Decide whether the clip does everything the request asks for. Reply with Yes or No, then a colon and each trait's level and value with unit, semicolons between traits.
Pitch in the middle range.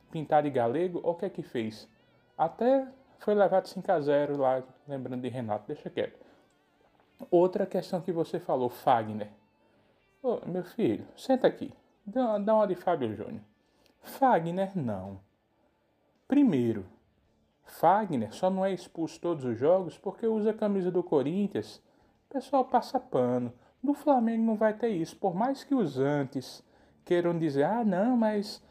Yes: medium, 180 Hz